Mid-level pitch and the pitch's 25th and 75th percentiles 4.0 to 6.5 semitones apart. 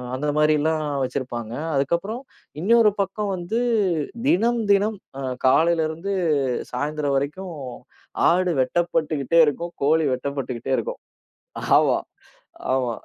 Yes: medium, 160 Hz; average, 5.1 semitones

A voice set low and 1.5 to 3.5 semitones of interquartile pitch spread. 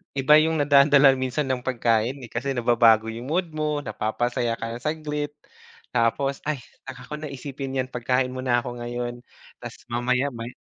Yes: low, 130 Hz; average, 2.8 semitones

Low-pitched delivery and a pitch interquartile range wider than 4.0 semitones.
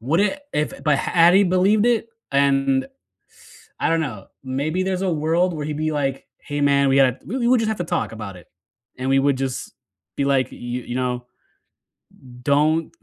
No: medium, 145 Hz; average, 4.9 semitones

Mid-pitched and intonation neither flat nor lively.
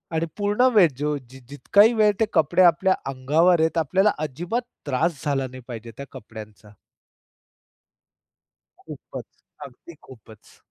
No: medium, 155 Hz; wide, 6.2 semitones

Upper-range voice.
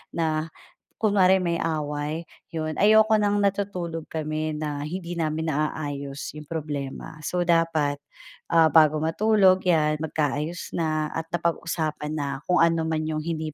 No: medium, 160 Hz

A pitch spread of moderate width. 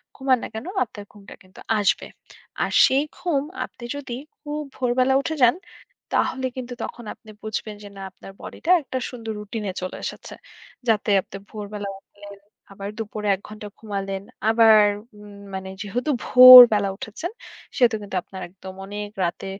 Yes: average, 3.7 semitones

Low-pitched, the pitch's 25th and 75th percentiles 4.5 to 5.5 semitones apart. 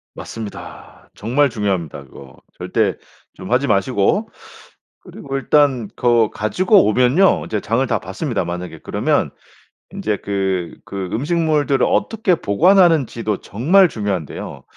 No: low, 115 Hz; wide, 7.1 semitones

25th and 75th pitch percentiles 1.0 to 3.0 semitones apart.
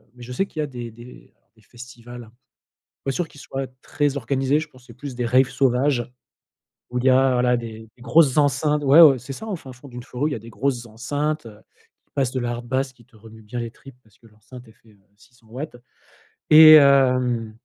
Yes: average, 2.7 semitones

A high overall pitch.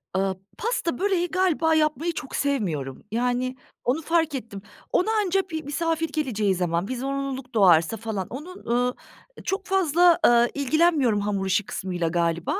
Yes: very high, 260 Hz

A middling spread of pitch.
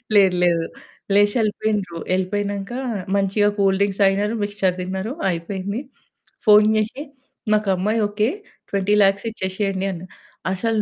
No: narrow, 1.7 semitones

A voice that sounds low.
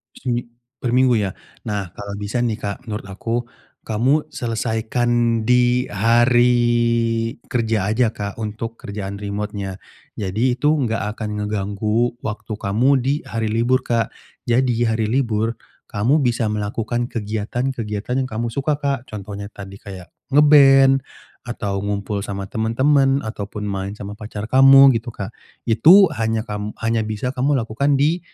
Yes: low, 115 Hz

